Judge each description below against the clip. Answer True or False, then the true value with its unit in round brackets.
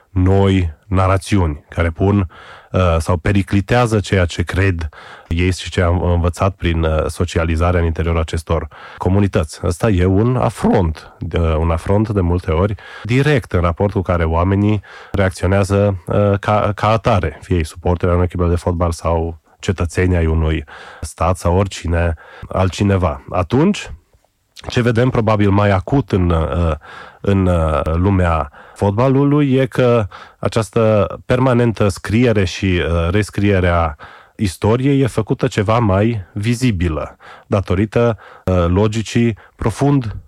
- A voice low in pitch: True (95 Hz)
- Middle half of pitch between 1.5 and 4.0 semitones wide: True (3.7 semitones)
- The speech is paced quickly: False (125 wpm)